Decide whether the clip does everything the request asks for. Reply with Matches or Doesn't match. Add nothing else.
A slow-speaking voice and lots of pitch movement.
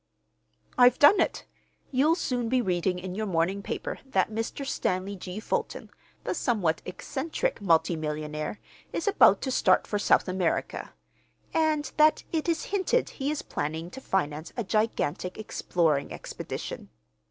Doesn't match